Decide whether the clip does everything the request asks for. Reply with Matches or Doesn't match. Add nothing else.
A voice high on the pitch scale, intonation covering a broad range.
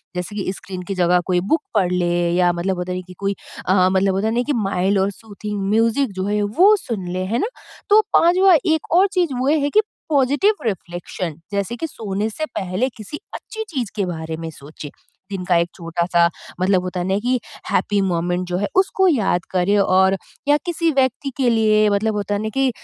Matches